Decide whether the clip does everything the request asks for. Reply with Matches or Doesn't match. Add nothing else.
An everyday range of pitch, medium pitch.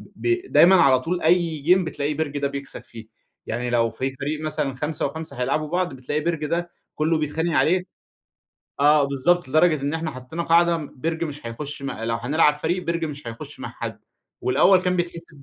Matches